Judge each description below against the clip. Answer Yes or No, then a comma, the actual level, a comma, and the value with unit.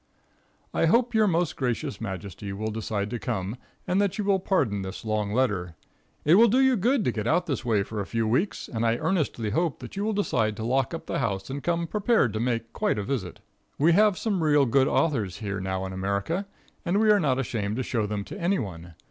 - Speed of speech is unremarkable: No, fast, 230 wpm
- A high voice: No, low, 125 Hz